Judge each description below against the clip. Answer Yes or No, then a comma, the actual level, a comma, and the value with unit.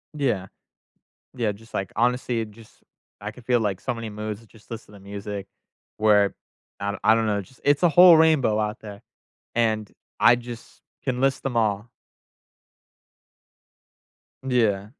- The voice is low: Yes, low, 110 Hz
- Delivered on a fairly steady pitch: No, average, 3.1 semitones